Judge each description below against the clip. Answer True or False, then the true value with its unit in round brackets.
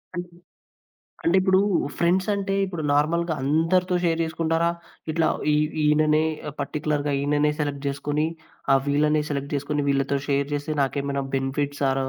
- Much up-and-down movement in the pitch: False (2.7 semitones)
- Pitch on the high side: False (150 Hz)